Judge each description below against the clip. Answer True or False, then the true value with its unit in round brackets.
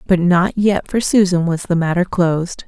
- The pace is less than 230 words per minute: True (200 wpm)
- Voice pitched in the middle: True (180 Hz)